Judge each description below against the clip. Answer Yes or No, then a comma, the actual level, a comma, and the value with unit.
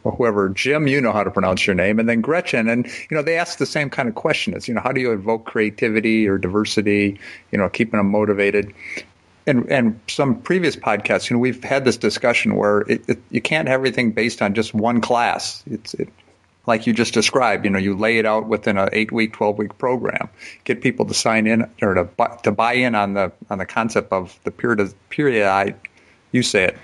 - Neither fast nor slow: No, fast, 235 wpm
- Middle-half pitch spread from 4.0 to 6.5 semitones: No, average, 2.7 semitones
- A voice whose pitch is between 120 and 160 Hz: No, low, 110 Hz